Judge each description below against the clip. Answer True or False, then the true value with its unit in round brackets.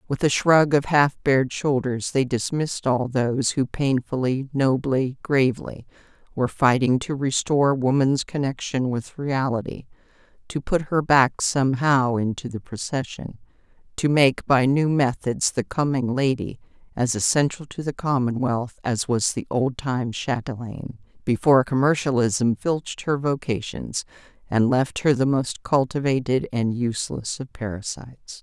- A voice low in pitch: True (130 Hz)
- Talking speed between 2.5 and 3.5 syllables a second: False (4.5 syllables/s)